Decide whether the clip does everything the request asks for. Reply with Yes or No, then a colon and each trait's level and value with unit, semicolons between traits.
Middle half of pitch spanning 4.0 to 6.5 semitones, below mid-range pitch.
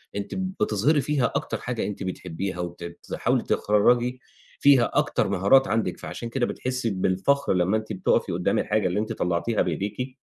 Yes: average, 5.2 semitones; low, 110 Hz